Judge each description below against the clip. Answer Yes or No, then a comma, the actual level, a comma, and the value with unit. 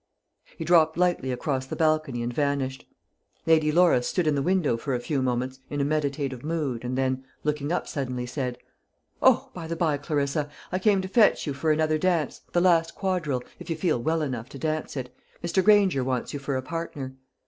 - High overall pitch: No, medium, 150 Hz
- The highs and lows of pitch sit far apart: No, average, 3.9 semitones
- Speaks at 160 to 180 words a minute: No, fast, 205 wpm